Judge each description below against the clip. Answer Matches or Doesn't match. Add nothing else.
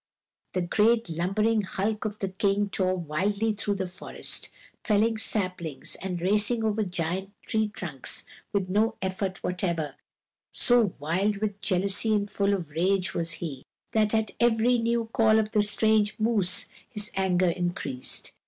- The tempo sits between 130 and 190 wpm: Matches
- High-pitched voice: Matches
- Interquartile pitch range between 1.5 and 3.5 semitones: Matches